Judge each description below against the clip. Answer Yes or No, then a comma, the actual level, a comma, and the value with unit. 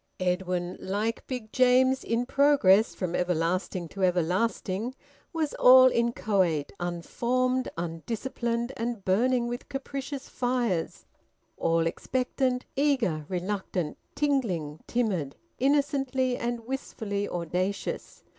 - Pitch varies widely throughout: Yes, wide, 6.1 semitones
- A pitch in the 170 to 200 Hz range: No, high, 230 Hz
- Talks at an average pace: No, slow, 100 wpm